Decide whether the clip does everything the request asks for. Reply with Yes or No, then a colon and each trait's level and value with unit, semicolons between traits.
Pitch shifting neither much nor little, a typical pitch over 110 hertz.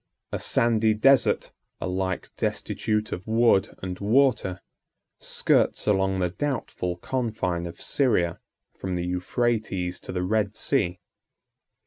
No: average, 4.1 semitones; very low, 95 Hz